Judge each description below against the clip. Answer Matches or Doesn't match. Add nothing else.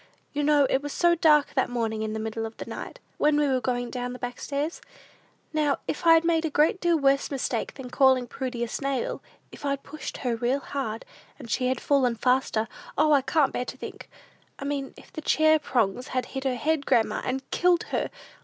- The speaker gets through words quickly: Matches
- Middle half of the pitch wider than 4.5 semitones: Doesn't match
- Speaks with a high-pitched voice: Matches